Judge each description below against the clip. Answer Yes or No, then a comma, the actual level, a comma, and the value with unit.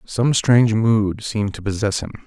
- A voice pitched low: Yes, low, 110 Hz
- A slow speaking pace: No, average, 185 wpm